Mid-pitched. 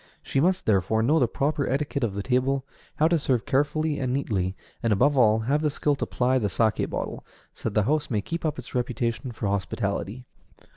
No: low, 125 Hz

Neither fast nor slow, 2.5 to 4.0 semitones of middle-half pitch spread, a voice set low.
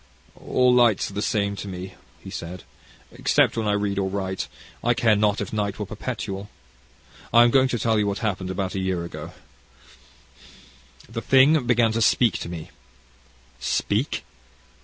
Yes: average, 170 wpm; average, 3.5 semitones; low, 105 Hz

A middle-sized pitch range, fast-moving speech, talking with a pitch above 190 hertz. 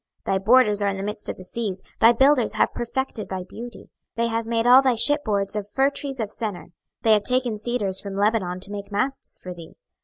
Yes: average, 3.5 semitones; fast, 240 wpm; high, 220 Hz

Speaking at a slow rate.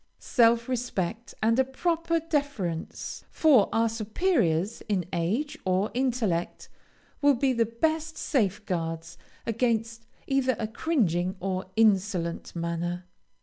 Yes: slow, 110 wpm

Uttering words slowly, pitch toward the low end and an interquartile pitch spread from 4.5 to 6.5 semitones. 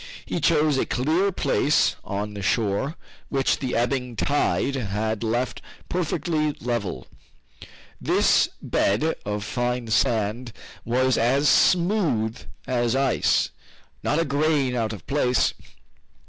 Yes: slow, 120 wpm; low, 125 Hz; average, 4.8 semitones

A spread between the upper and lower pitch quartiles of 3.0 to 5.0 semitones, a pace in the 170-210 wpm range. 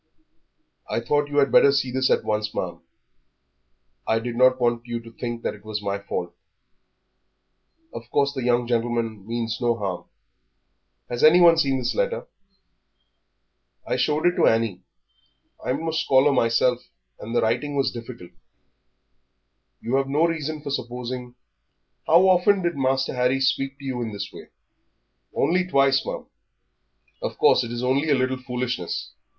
No: average, 3.3 semitones; average, 155 wpm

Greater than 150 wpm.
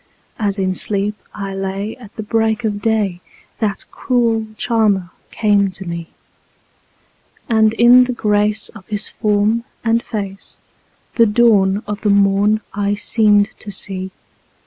No: slow, 135 wpm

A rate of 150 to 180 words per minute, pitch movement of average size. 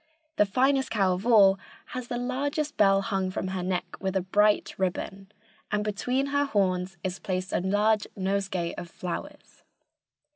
Yes: average, 160 wpm; average, 4.3 semitones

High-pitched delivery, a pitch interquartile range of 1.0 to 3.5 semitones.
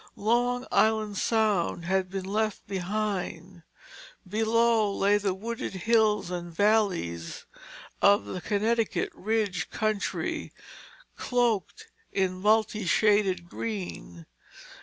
Yes: high, 205 Hz; average, 3.1 semitones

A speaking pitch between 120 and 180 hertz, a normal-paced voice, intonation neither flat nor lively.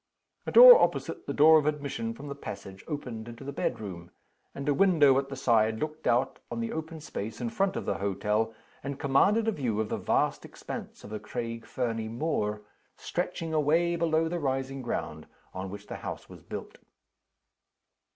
No: low, 135 Hz; average, 185 wpm; wide, 6.1 semitones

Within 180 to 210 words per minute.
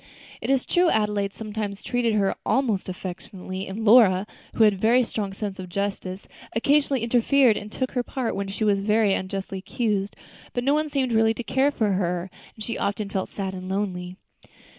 Yes: average, 190 wpm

